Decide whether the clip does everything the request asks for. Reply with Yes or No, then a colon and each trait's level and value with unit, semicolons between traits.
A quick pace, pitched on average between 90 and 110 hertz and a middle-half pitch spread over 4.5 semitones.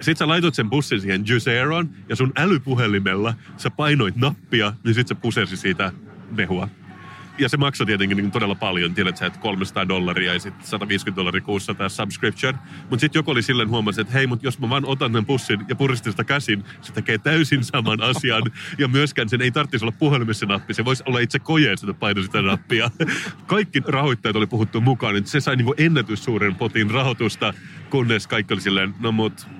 No: fast, 195 wpm; low, 120 Hz; average, 5.1 semitones